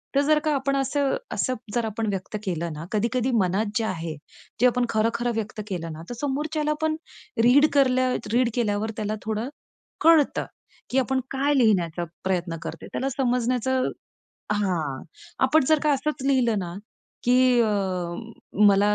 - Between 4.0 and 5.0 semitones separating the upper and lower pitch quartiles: Yes, average, 4.7 semitones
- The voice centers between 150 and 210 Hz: No, high, 240 Hz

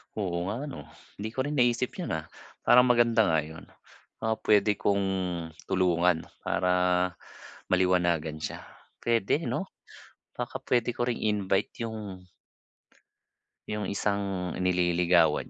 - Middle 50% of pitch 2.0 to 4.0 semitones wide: No, average, 4.4 semitones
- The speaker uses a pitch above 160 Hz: No, very low, 95 Hz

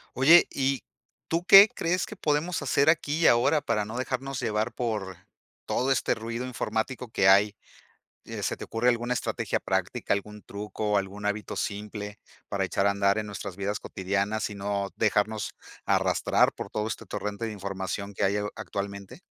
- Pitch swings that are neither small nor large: Yes, average, 3.8 semitones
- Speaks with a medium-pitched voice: No, low, 105 Hz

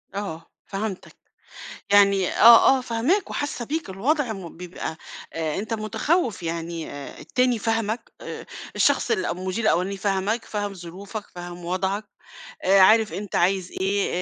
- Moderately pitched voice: No, high, 200 Hz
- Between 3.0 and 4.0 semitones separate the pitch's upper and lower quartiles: Yes, average, 3.7 semitones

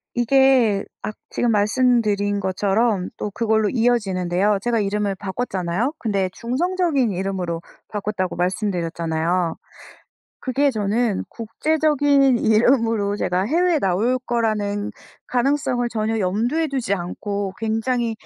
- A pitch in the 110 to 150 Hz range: No, high, 215 Hz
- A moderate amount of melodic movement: Yes, average, 3.8 semitones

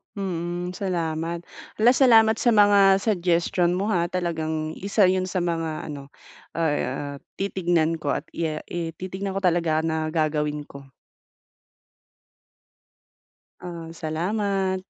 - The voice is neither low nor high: Yes, medium, 175 Hz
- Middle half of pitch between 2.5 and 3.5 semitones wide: Yes, average, 3.2 semitones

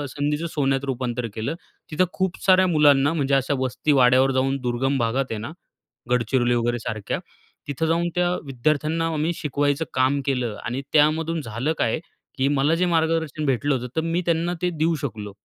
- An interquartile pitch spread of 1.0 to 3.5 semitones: No, average, 4.1 semitones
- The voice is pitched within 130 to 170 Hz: Yes, medium, 140 Hz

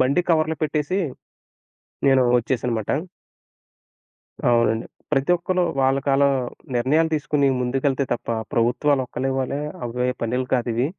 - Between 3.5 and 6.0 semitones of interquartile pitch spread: No, average, 3.0 semitones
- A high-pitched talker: No, low, 135 Hz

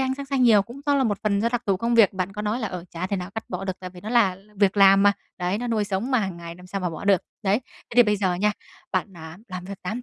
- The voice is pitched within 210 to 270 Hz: No, high, 200 Hz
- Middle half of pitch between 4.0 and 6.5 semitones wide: No, average, 3.5 semitones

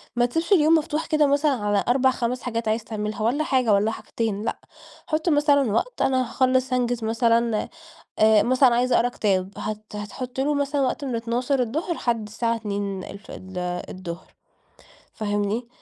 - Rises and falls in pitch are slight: No, average, 3.9 semitones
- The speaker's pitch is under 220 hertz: No, high, 235 Hz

